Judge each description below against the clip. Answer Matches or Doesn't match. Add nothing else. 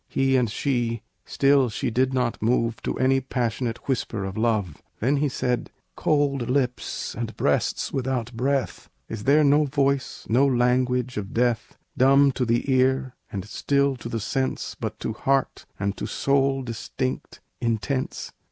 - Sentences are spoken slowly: Doesn't match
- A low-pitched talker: Matches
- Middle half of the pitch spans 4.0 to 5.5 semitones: Doesn't match